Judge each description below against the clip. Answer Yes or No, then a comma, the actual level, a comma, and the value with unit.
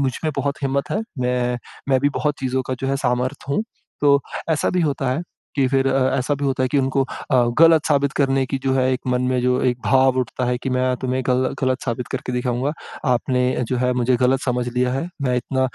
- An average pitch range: No, narrow, 1.5 semitones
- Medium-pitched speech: No, low, 130 Hz